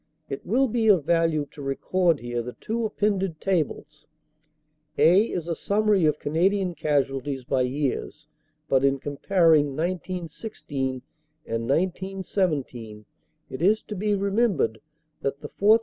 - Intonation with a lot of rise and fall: Yes, wide, 5.9 semitones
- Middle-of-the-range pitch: Yes, medium, 165 Hz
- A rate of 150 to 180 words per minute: No, slow, 135 wpm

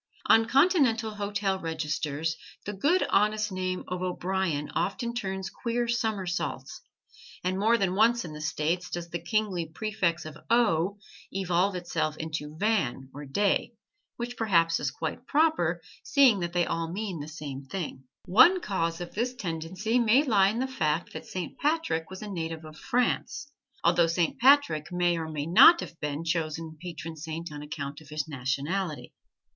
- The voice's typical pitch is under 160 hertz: No, medium, 180 Hz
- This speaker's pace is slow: No, average, 160 wpm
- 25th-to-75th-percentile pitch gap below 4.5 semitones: No, average, 5.2 semitones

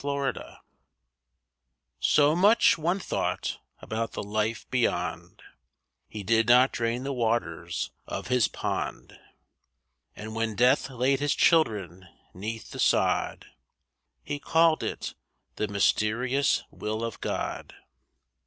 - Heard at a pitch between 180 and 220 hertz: No, low, 120 Hz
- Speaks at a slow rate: Yes, slow, 115 wpm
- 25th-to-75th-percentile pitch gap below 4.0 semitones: No, average, 4.5 semitones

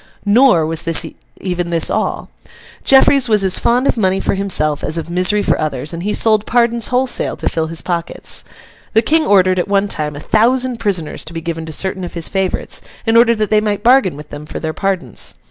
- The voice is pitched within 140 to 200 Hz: Yes, high, 190 Hz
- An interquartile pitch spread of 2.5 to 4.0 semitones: No, average, 5.3 semitones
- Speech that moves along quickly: Yes, fast, 215 wpm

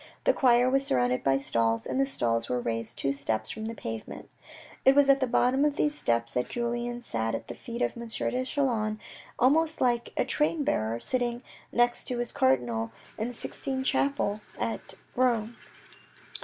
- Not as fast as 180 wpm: No, average, 185 wpm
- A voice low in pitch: No, high, 235 Hz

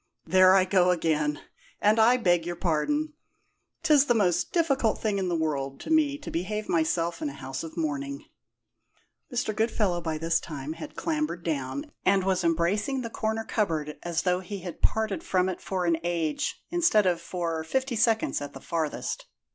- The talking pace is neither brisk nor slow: Yes, average, 180 wpm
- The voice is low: No, medium, 180 Hz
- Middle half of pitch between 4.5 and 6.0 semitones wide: Yes, average, 5.2 semitones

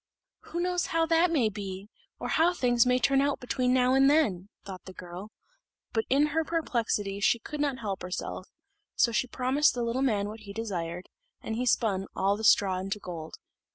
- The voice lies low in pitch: No, high, 230 Hz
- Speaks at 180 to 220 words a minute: Yes, average, 195 wpm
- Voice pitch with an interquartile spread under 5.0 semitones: No, wide, 5.6 semitones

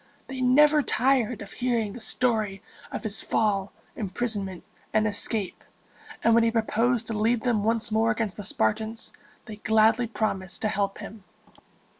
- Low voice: No, high, 220 Hz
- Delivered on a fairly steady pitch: Yes, narrow, 2.2 semitones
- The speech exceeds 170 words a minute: No, average, 155 wpm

